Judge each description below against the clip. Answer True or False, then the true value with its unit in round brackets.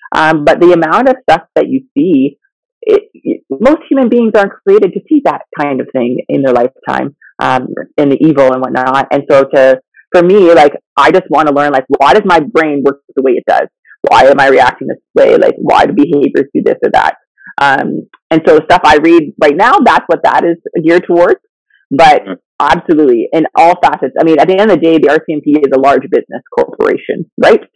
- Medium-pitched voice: True (175 Hz)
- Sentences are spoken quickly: True (220 wpm)